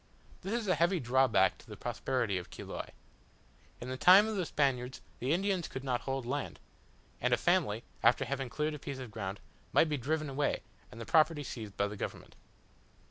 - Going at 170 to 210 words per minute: Yes, average, 195 wpm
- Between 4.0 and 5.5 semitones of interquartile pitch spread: Yes, average, 4.4 semitones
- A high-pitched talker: No, low, 135 Hz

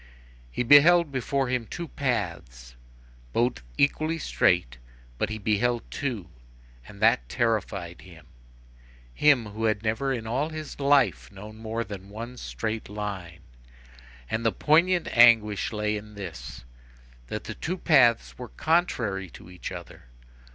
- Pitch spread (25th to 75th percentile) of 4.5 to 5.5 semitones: Yes, average, 5.1 semitones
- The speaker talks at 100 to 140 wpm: Yes, slow, 135 wpm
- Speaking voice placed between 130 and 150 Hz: No, low, 110 Hz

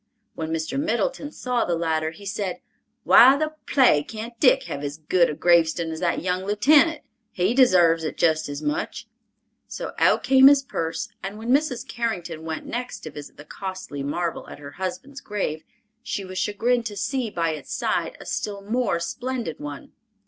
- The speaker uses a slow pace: No, average, 180 wpm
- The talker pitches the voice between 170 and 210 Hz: Yes, high, 190 Hz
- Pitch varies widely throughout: Yes, wide, 7.4 semitones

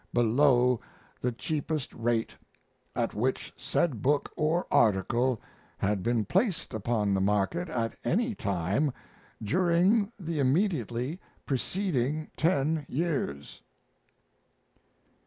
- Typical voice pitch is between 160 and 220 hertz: No, low, 130 Hz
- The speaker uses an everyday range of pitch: No, wide, 6.5 semitones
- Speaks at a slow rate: Yes, slow, 100 wpm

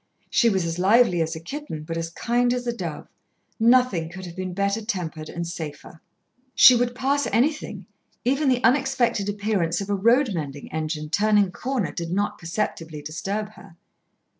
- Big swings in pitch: Yes, wide, 6.5 semitones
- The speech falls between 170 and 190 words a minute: Yes, average, 175 wpm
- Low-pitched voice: No, high, 200 Hz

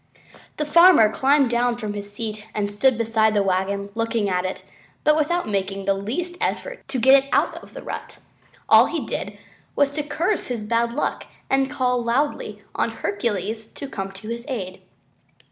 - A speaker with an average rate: Yes, average, 180 wpm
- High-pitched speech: Yes, high, 230 Hz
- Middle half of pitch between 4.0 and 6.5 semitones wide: Yes, average, 5.1 semitones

